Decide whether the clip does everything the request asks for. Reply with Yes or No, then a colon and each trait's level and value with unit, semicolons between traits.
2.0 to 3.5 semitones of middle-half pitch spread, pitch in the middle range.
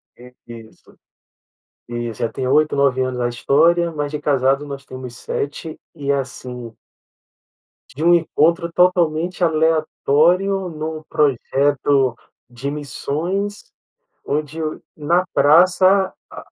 No: average, 4.1 semitones; medium, 150 Hz